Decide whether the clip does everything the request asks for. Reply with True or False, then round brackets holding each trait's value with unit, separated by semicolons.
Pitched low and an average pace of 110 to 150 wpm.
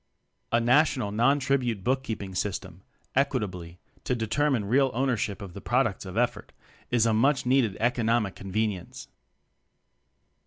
True (115 Hz; 140 wpm)